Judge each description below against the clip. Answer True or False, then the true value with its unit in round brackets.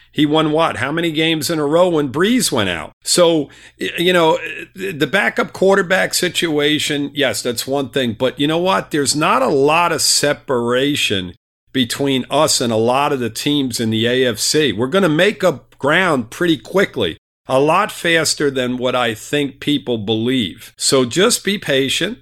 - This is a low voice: False (145 Hz)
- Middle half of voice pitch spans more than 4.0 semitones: True (4.6 semitones)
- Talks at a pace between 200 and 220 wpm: False (180 wpm)